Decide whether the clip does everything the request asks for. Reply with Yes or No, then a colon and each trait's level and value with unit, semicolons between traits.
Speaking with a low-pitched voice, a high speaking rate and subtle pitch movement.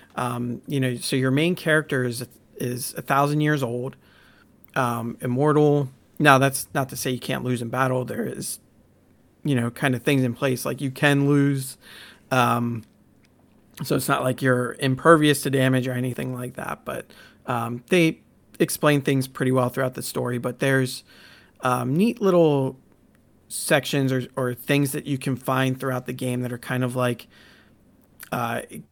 No: low, 130 Hz; average, 170 wpm; narrow, 2.2 semitones